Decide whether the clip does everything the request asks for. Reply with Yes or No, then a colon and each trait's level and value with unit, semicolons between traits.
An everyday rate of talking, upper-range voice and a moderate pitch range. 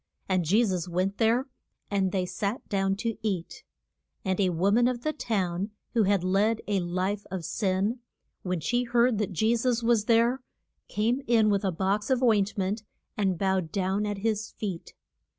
Yes: average, 185 wpm; high, 205 Hz; average, 3.3 semitones